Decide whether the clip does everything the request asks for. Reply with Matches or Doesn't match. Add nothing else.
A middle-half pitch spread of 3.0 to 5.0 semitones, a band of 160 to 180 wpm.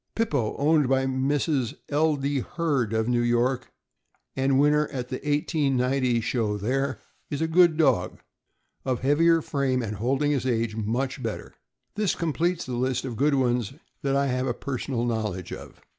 Matches